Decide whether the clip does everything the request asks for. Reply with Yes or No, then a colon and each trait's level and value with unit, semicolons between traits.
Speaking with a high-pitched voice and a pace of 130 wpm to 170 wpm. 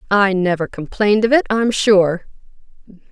Yes: high, 200 Hz; slow, 135 wpm